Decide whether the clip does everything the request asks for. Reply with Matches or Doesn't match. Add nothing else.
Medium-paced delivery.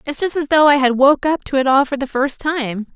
Doesn't match